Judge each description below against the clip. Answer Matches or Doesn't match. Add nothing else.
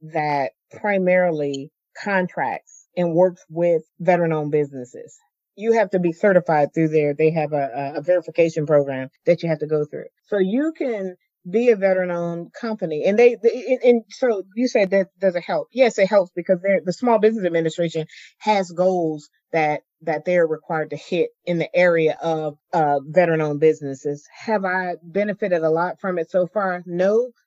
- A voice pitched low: Doesn't match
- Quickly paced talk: Doesn't match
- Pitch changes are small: Doesn't match